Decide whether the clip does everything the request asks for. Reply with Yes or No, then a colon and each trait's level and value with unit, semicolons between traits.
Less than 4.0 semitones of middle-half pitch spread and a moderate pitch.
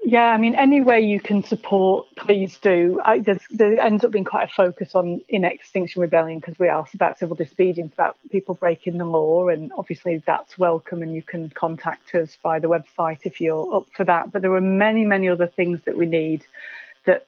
Yes: average, 3.1 semitones; medium, 180 Hz